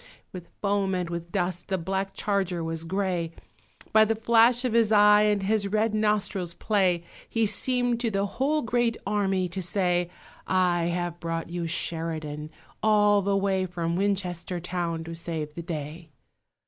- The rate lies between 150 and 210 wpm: Yes, average, 160 wpm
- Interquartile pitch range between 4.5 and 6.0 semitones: No, average, 3.5 semitones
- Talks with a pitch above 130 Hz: Yes, high, 190 Hz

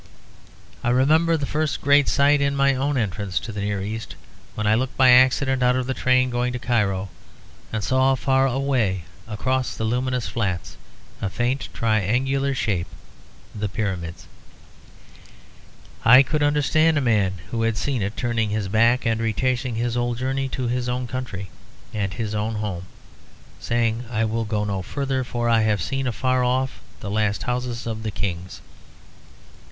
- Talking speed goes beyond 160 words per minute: Yes, average, 170 wpm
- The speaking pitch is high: No, low, 120 Hz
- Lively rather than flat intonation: No, average, 3.6 semitones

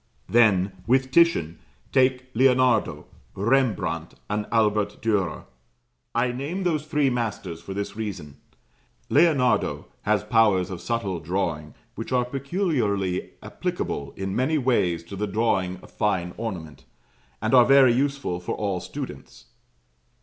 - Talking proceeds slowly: Yes, slow, 130 wpm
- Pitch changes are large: Yes, wide, 5.7 semitones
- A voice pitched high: No, low, 110 Hz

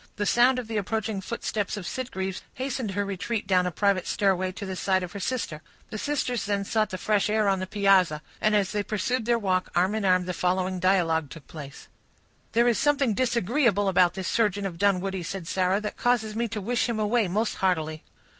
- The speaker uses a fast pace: Yes, fast, 210 wpm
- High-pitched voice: Yes, high, 200 Hz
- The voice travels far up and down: No, average, 3.3 semitones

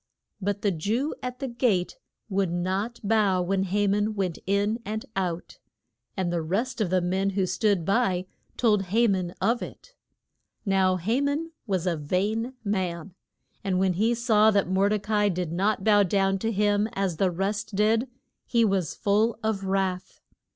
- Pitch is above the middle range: Yes, high, 200 Hz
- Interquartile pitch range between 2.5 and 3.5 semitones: Yes, average, 2.8 semitones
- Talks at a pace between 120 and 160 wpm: No, average, 175 wpm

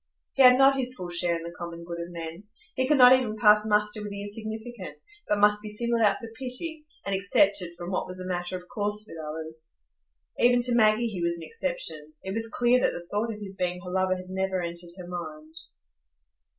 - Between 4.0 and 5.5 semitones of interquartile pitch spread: Yes, average, 4.6 semitones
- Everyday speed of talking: No, fast, 225 wpm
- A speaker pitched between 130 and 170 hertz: No, high, 200 Hz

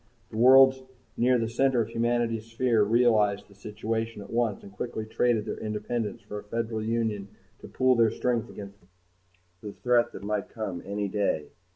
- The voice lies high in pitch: No, low, 110 Hz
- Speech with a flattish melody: Yes, narrow, 2.3 semitones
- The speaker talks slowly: No, average, 175 wpm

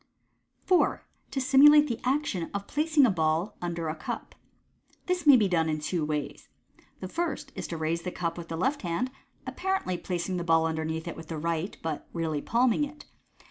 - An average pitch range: No, wide, 8.4 semitones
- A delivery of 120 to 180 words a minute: No, average, 195 wpm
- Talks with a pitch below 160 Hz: No, medium, 175 Hz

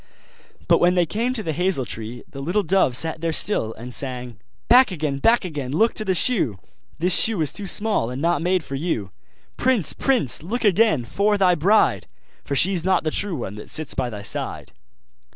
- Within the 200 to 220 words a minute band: Yes, fast, 205 wpm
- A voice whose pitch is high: No, medium, 170 Hz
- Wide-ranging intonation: Yes, wide, 7.0 semitones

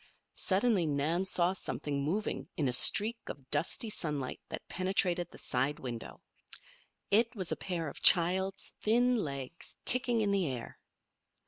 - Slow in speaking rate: No, average, 145 wpm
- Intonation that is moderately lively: No, wide, 6.1 semitones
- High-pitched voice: No, medium, 180 Hz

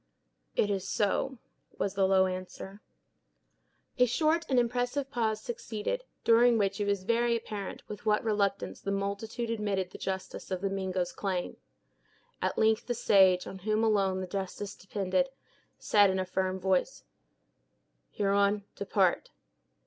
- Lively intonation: No, average, 3.1 semitones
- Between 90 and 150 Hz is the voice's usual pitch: No, high, 200 Hz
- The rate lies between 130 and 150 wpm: Yes, average, 145 wpm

